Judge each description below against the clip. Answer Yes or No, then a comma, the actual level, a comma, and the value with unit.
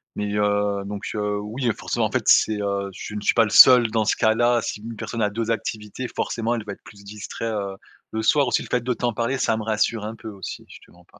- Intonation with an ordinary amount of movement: No, narrow, 2.0 semitones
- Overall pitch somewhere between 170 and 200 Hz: No, low, 110 Hz